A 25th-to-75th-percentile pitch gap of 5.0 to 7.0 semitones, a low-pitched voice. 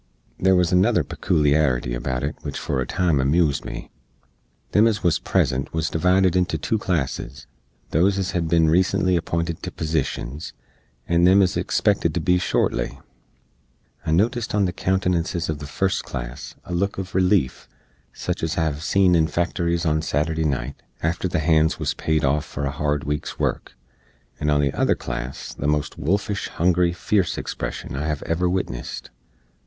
No: average, 3.7 semitones; very low, 80 Hz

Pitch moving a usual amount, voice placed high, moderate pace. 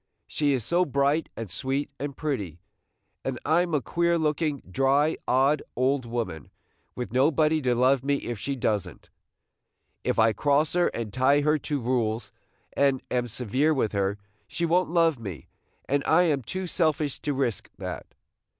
No: average, 4.0 semitones; medium, 140 Hz; average, 170 wpm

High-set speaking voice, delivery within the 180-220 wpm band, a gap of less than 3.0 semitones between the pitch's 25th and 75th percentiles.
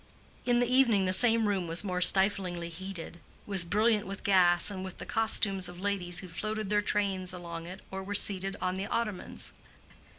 Yes: high, 195 Hz; average, 190 wpm; narrow, 2.4 semitones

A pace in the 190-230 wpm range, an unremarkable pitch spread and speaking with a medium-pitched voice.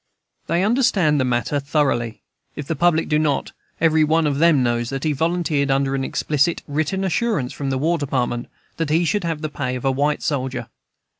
Yes: average, 200 wpm; average, 3.4 semitones; medium, 150 Hz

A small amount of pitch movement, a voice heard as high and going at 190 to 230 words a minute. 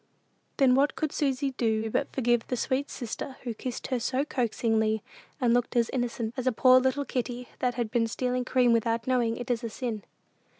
Yes: narrow, 2.0 semitones; high, 245 Hz; average, 200 wpm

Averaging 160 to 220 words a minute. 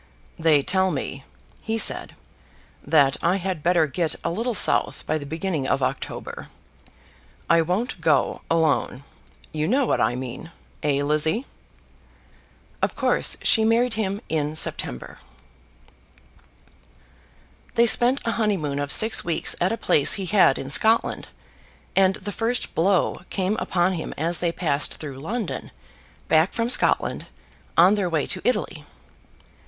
No: average, 140 wpm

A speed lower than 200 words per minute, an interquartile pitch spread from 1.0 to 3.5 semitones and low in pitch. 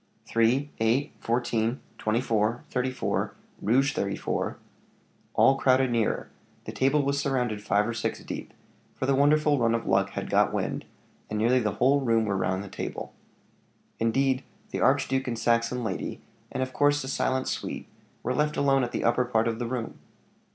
Yes: average, 180 wpm; average, 2.9 semitones; low, 125 Hz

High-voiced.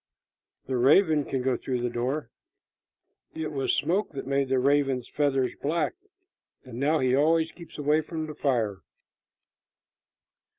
No: medium, 140 Hz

